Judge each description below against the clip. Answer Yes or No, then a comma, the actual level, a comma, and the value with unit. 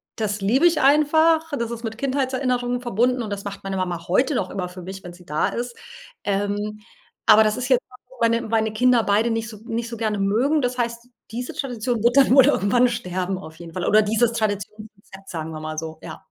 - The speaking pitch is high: Yes, high, 225 Hz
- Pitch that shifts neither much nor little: Yes, average, 4.0 semitones